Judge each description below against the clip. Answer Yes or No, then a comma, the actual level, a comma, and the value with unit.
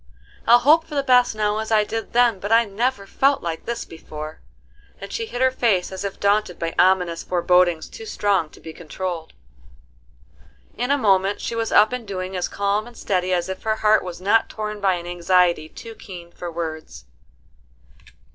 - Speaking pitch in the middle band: No, high, 200 Hz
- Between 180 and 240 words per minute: Yes, average, 195 wpm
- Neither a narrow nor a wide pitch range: Yes, average, 4.2 semitones